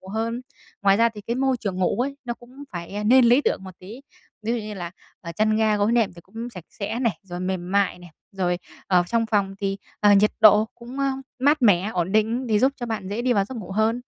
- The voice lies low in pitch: No, high, 215 Hz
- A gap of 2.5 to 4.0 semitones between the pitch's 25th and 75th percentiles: Yes, average, 3.6 semitones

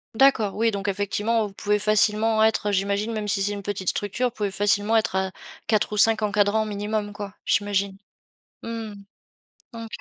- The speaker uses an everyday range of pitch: No, narrow, 1.4 semitones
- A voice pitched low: No, high, 210 Hz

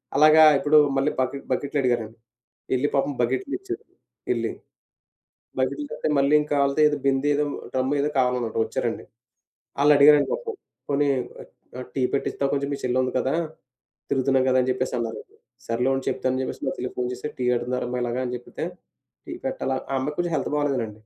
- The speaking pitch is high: No, low, 135 Hz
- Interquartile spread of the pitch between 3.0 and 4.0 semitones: No, narrow, 2.6 semitones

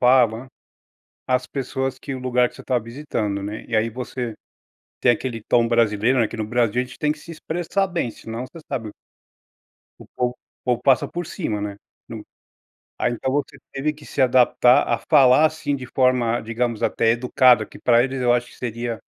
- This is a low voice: Yes, low, 125 Hz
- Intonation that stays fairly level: Yes, narrow, 2.3 semitones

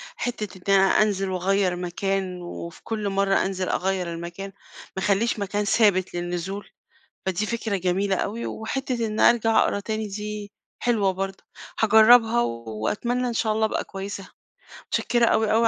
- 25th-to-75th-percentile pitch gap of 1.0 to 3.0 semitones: Yes, average, 2.7 semitones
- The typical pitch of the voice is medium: No, high, 200 Hz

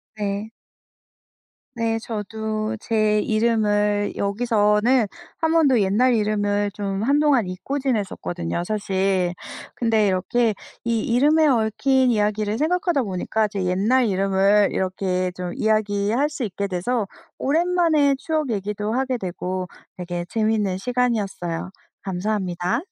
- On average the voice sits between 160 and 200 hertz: No, high, 215 Hz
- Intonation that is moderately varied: Yes, average, 3.8 semitones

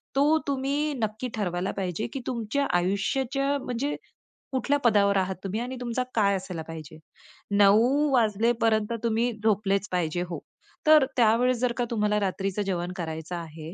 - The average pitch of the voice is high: Yes, high, 215 Hz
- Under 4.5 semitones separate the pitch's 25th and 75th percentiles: No, average, 4.9 semitones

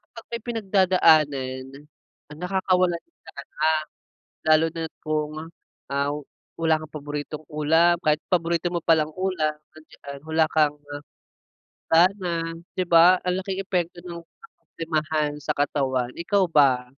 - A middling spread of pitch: Yes, average, 3.1 semitones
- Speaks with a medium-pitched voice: Yes, medium, 165 Hz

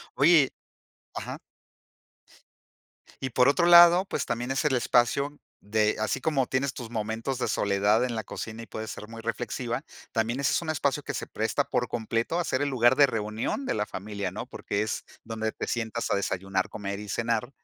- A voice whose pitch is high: No, low, 115 Hz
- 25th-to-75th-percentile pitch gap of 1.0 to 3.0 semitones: No, average, 3.7 semitones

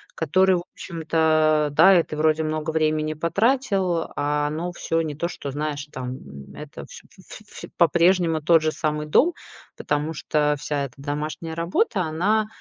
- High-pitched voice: No, medium, 155 Hz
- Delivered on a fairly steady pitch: Yes, narrow, 2.3 semitones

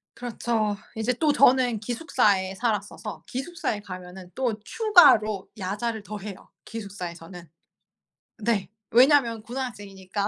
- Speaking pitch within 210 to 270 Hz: Yes, high, 215 Hz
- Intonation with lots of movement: No, average, 3.9 semitones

